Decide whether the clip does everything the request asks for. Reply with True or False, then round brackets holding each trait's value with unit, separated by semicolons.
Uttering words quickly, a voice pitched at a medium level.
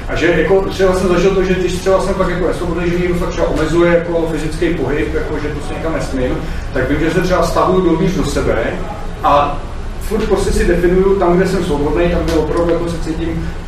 True (230 wpm; 175 Hz)